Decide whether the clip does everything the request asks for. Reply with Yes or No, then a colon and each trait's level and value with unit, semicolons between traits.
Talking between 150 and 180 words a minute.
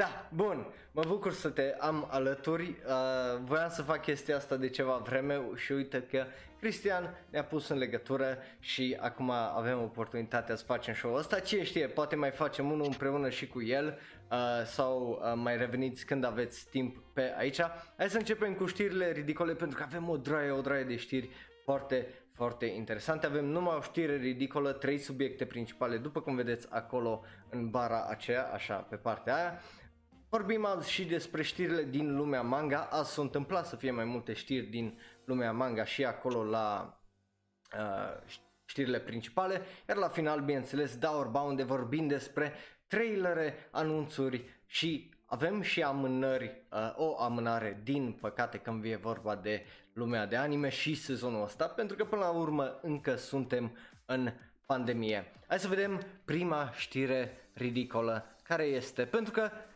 Yes: average, 165 wpm